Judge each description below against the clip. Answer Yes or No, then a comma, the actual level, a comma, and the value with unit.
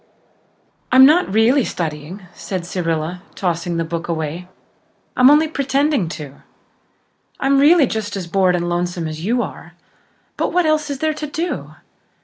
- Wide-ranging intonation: Yes, wide, 8.6 semitones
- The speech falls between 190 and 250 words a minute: No, average, 150 wpm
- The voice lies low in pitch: No, high, 195 Hz